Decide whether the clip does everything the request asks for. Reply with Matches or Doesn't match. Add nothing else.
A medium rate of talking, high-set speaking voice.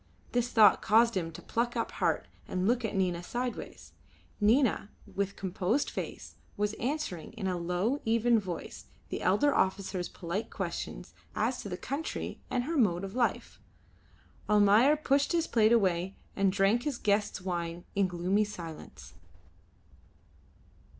Matches